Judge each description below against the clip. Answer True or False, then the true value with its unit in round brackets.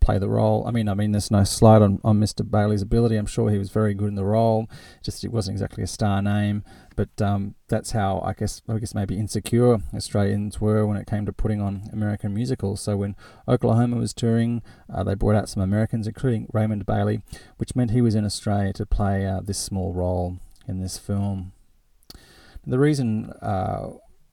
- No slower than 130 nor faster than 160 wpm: False (205 wpm)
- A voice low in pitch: True (105 Hz)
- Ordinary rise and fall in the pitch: False (1.9 semitones)